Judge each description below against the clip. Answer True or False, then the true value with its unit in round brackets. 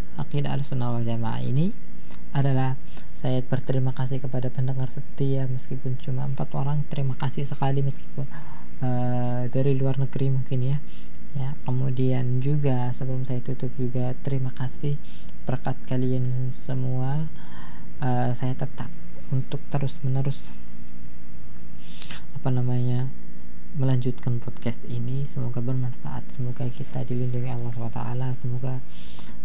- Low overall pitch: True (130 Hz)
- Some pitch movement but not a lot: False (1.5 semitones)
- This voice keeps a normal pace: True (110 wpm)